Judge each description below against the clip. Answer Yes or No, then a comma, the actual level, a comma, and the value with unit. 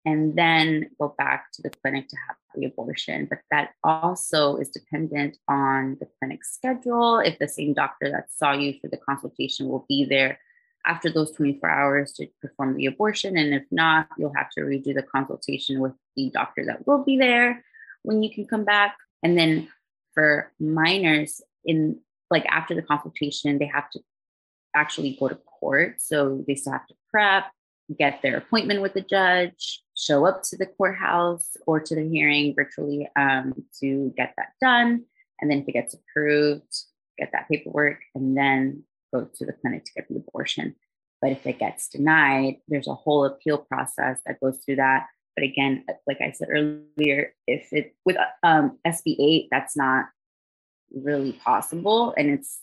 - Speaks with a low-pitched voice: No, medium, 150 Hz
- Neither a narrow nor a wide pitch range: Yes, average, 4.0 semitones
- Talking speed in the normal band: Yes, average, 175 wpm